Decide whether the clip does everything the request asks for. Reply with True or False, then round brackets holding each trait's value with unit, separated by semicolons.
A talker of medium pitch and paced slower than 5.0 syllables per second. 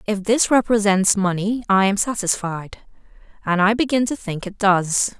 False (205 Hz; 4.5 syllables/s)